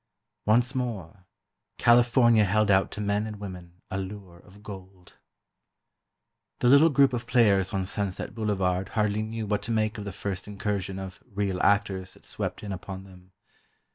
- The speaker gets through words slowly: No, average, 165 wpm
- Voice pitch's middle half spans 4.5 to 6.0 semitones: No, narrow, 2.5 semitones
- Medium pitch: No, low, 100 Hz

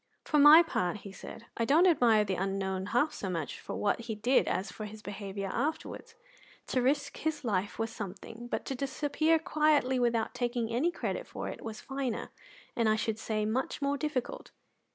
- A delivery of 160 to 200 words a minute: Yes, average, 190 wpm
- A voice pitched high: Yes, high, 235 Hz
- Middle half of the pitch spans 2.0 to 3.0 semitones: No, average, 5.2 semitones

